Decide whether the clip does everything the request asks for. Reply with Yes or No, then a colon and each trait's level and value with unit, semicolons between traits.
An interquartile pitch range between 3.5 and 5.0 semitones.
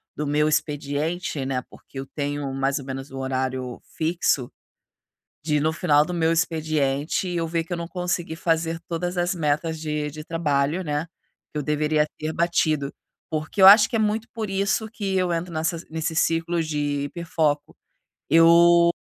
No: average, 2.8 semitones